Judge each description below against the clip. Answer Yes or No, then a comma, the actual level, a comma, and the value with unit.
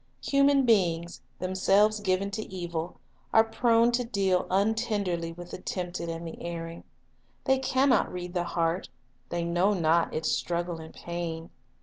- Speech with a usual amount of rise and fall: Yes, average, 4.1 semitones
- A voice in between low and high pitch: Yes, medium, 180 Hz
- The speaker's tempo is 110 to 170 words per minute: Yes, average, 155 wpm